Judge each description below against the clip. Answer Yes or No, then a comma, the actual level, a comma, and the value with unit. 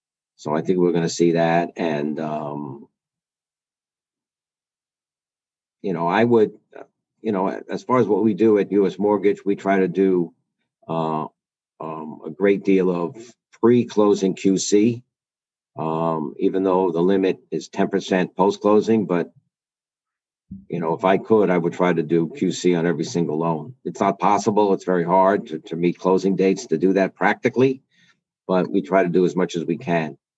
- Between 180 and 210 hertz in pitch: No, very low, 95 Hz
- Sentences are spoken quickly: No, average, 175 wpm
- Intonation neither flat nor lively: Yes, average, 3.1 semitones